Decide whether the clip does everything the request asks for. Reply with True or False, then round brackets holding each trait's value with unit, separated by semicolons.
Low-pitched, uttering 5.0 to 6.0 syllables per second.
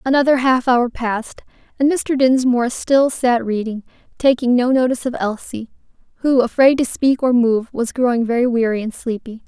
False (245 Hz; 5.2 syllables/s)